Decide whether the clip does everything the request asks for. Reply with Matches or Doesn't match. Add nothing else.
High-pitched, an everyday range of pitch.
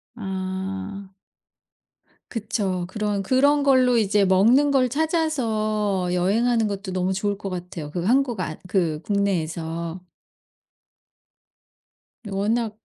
Matches